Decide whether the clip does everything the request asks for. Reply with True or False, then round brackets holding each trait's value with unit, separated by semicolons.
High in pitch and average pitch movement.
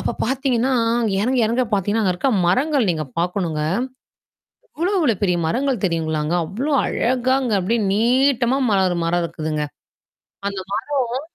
False (220 Hz; 6.6 semitones)